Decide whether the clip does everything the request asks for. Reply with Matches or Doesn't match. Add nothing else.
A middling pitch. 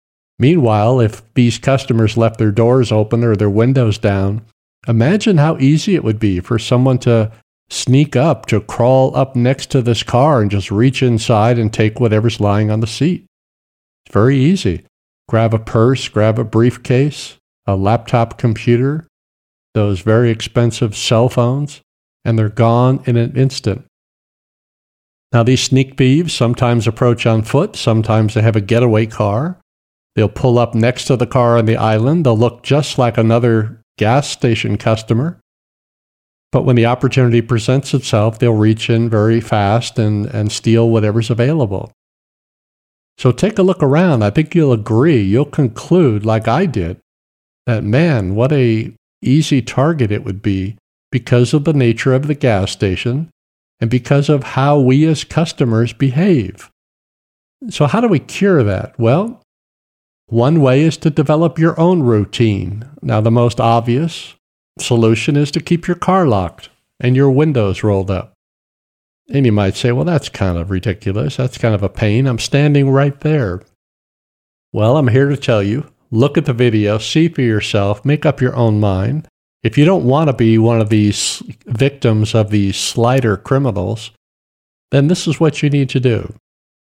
Doesn't match